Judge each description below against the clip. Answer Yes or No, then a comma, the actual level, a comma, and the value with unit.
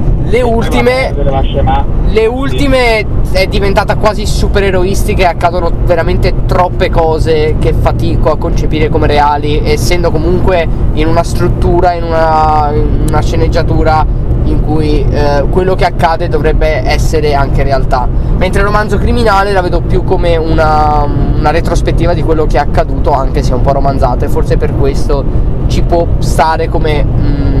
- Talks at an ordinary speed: Yes, average, 150 wpm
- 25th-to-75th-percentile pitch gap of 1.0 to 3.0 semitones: No, average, 3.4 semitones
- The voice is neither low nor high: Yes, medium, 150 Hz